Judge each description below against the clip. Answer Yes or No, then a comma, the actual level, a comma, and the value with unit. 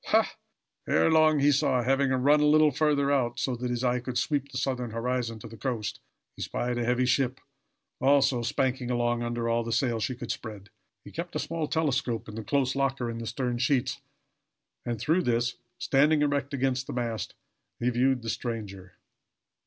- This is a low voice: Yes, low, 125 Hz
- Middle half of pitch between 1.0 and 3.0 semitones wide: Yes, narrow, 2.6 semitones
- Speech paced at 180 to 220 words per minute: Yes, average, 190 wpm